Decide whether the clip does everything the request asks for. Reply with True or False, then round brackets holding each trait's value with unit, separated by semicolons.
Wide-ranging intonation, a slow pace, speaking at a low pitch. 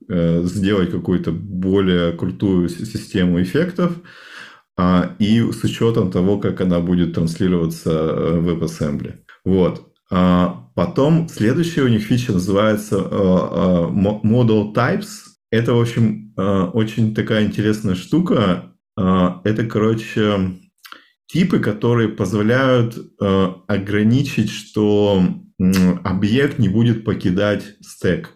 False (3.6 semitones; 95 wpm; 105 Hz)